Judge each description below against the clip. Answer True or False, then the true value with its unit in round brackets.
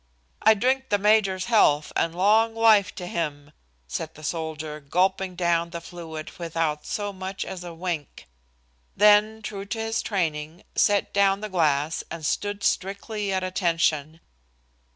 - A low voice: False (185 Hz)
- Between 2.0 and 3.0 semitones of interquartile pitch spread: False (4.0 semitones)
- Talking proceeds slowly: False (150 wpm)